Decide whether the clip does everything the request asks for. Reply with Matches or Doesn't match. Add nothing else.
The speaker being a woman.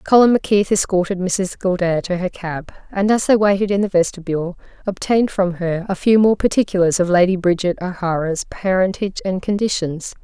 Matches